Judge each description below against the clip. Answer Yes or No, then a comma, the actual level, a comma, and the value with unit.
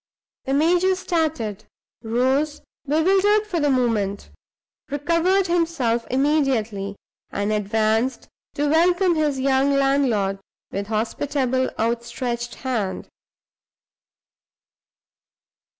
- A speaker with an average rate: No, slow, 85 wpm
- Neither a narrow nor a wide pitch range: No, wide, 5.9 semitones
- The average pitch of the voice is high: Yes, very high, 265 Hz